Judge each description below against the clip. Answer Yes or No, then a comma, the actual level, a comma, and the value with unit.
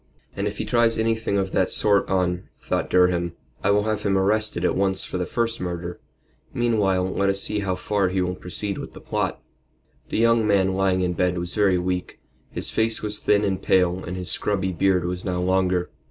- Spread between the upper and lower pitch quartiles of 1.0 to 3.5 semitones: Yes, narrow, 2.4 semitones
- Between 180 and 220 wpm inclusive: Yes, fast, 205 wpm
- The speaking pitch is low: Yes, very low, 95 Hz